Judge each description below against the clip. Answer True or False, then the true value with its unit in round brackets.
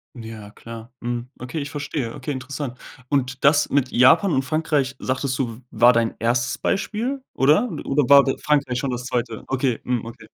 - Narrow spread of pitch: False (3.0 semitones)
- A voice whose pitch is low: True (130 Hz)